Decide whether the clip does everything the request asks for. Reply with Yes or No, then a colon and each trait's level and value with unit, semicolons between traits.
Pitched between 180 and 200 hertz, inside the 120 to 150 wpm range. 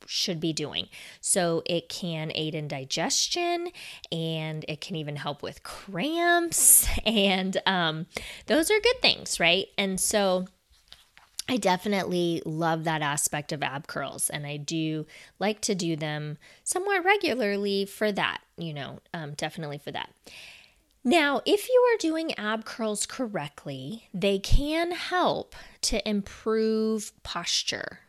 Yes: medium, 185 Hz; slow, 135 wpm